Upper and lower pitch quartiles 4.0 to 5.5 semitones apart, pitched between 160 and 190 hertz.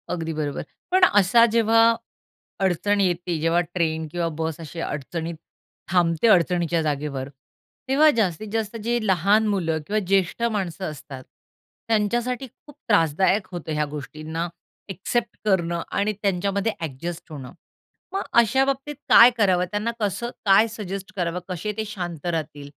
Yes: average, 4.6 semitones; medium, 185 Hz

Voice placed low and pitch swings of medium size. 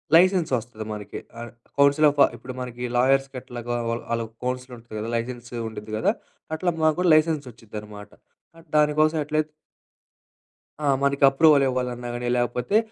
Yes: low, 125 Hz; average, 4.2 semitones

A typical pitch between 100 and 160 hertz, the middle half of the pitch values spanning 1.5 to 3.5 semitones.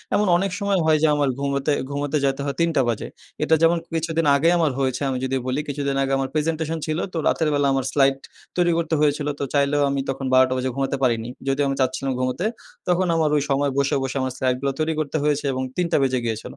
Yes: medium, 140 Hz; average, 2.9 semitones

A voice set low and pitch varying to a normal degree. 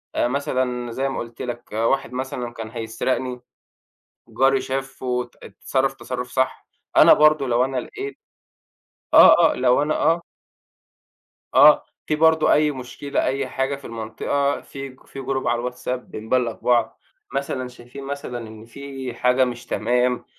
No: low, 130 Hz; narrow, 2.1 semitones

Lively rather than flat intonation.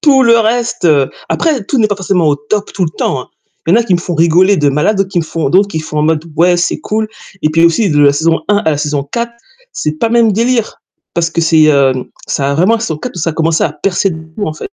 Yes: wide, 5.7 semitones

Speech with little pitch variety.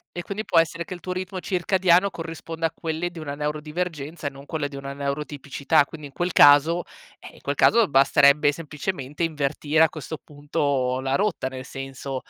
No: average, 3.2 semitones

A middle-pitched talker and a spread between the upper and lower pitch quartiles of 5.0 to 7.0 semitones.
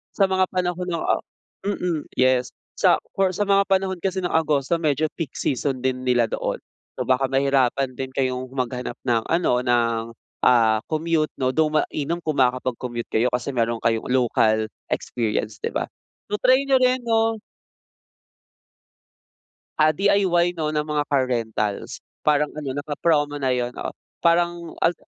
Yes: medium, 145 Hz; wide, 5.5 semitones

